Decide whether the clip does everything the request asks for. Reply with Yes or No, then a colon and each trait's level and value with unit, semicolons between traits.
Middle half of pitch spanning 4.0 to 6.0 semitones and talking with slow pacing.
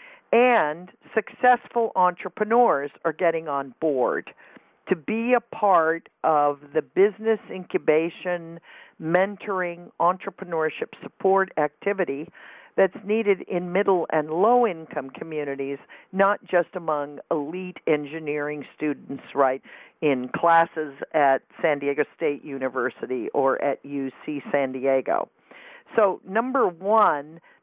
Yes: average, 5.1 semitones; slow, 105 wpm